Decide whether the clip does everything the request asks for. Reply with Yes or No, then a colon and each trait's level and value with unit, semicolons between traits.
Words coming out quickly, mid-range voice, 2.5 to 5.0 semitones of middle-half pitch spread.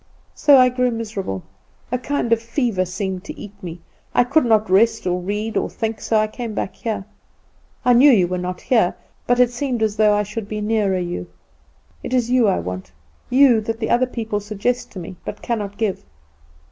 No: fast, 210 wpm; high, 220 Hz; average, 3.8 semitones